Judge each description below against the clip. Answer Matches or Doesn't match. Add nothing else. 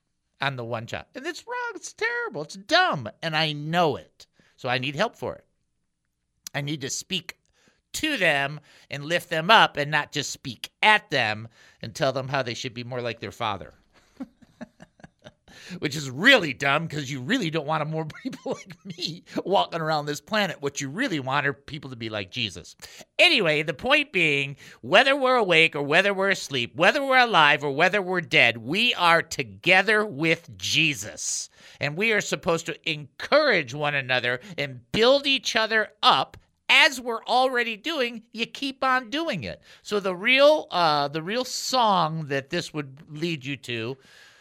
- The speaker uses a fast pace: Doesn't match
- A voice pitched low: Doesn't match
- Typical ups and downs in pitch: Doesn't match